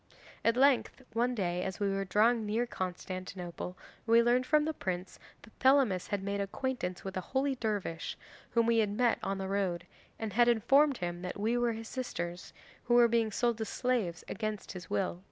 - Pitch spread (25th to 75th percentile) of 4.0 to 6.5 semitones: Yes, average, 4.5 semitones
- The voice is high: Yes, high, 215 Hz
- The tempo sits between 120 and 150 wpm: No, average, 190 wpm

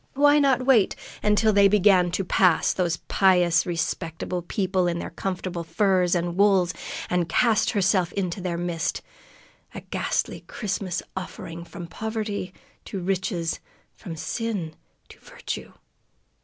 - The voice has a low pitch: No, medium, 185 Hz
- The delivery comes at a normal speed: No, slow, 130 wpm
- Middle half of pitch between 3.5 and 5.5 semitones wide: No, average, 3.0 semitones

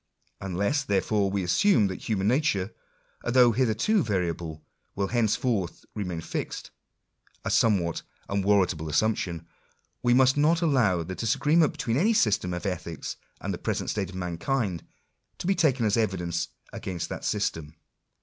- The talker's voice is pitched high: No, low, 100 Hz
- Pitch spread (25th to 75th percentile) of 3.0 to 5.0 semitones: No, wide, 5.5 semitones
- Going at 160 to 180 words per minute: No, average, 150 wpm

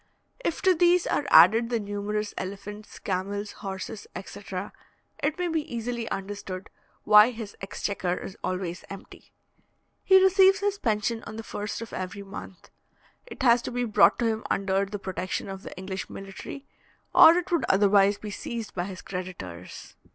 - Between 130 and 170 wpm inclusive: Yes, average, 165 wpm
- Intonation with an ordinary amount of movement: Yes, average, 3.7 semitones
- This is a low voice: No, high, 205 Hz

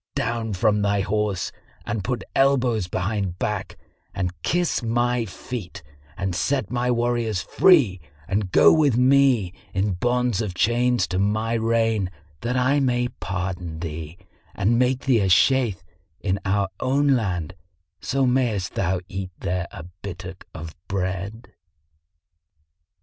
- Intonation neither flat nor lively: Yes, average, 4.7 semitones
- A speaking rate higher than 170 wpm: No, slow, 135 wpm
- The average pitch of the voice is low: Yes, low, 105 Hz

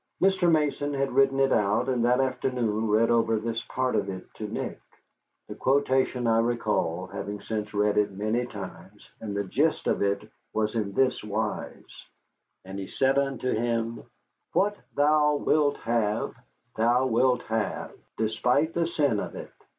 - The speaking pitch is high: No, low, 115 Hz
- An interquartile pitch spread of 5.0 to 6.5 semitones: No, average, 4.2 semitones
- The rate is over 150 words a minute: Yes, average, 160 wpm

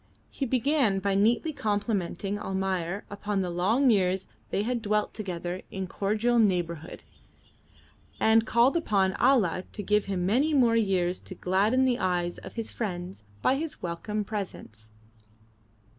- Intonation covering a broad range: No, average, 3.8 semitones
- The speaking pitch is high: Yes, high, 205 Hz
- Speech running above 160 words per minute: No, average, 145 wpm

